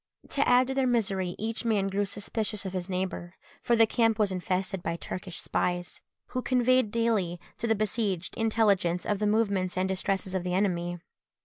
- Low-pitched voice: No, high, 200 Hz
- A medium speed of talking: Yes, average, 185 wpm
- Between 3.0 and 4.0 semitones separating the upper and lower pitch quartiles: Yes, average, 3.5 semitones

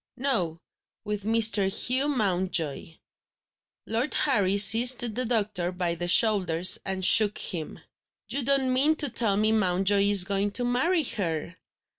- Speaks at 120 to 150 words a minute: Yes, average, 140 wpm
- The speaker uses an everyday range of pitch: Yes, average, 4.8 semitones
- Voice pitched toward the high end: Yes, high, 205 Hz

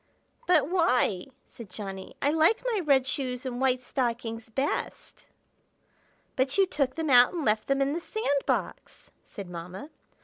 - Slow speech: No, average, 160 wpm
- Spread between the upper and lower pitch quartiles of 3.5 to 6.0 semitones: Yes, average, 4.7 semitones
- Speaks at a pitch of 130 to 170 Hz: No, very high, 265 Hz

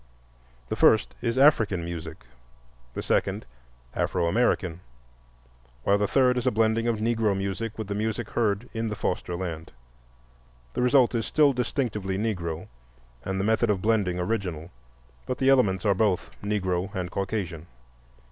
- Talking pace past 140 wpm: Yes, average, 150 wpm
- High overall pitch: No, low, 105 Hz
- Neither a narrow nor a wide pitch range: Yes, average, 3.7 semitones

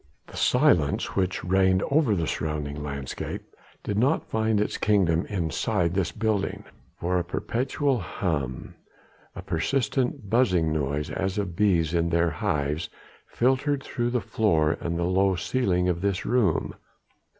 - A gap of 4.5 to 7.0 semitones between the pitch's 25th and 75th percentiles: Yes, average, 5.2 semitones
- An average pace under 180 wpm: Yes, average, 140 wpm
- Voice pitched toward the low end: Yes, very low, 95 Hz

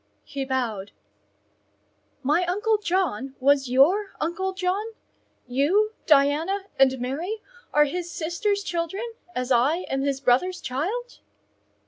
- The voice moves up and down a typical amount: No, wide, 6.1 semitones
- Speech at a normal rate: No, slow, 115 wpm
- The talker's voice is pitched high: Yes, very high, 320 Hz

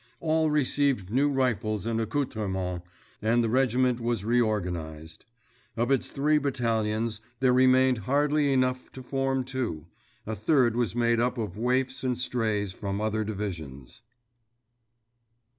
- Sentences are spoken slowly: Yes, slow, 125 wpm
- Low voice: Yes, low, 120 Hz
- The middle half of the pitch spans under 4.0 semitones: Yes, average, 3.6 semitones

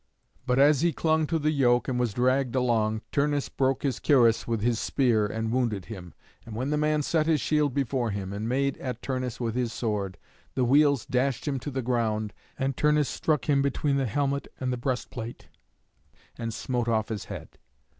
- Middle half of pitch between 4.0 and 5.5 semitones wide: No, average, 3.6 semitones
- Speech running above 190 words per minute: Yes, average, 200 wpm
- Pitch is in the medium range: No, low, 125 Hz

